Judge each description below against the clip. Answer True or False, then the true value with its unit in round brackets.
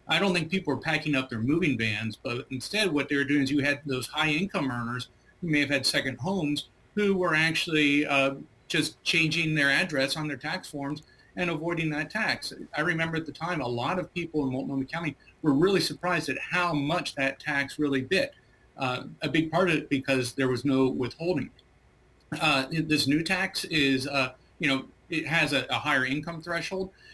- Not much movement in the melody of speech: False (3.5 semitones)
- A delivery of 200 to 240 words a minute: True (205 wpm)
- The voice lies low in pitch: False (150 Hz)